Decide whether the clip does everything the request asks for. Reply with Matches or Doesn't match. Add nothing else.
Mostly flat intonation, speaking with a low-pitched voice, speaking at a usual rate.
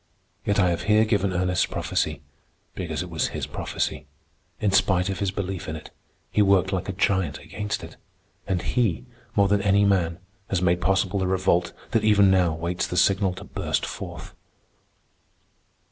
Matches